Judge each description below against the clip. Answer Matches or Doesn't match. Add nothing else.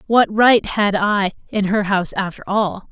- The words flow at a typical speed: Matches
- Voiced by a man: Doesn't match